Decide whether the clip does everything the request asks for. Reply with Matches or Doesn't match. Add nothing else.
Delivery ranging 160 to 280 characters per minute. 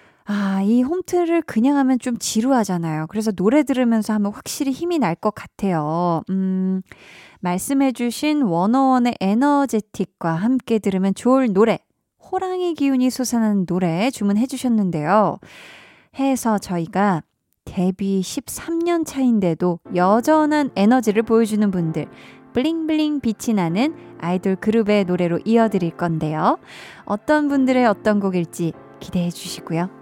Doesn't match